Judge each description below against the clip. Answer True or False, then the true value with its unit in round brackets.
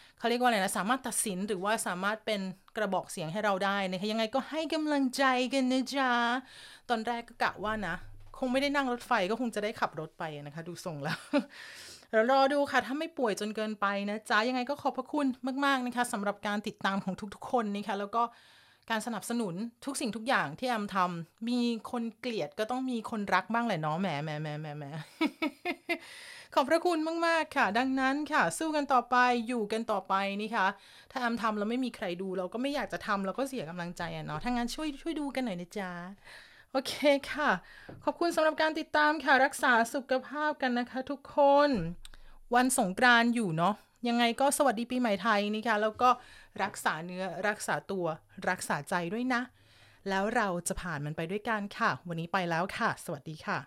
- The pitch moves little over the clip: False (5.1 semitones)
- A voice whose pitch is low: False (230 Hz)